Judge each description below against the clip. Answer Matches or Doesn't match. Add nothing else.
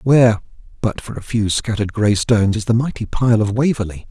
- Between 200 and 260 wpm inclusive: Matches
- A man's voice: Matches